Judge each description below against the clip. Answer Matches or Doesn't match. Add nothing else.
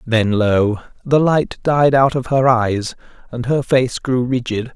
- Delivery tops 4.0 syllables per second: Doesn't match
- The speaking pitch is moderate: Doesn't match